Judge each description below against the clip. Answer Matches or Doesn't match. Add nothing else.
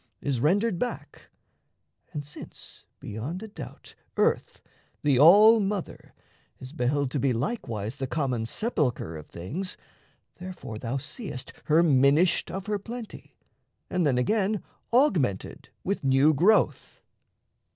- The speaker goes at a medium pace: Doesn't match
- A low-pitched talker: Doesn't match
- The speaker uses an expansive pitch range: Matches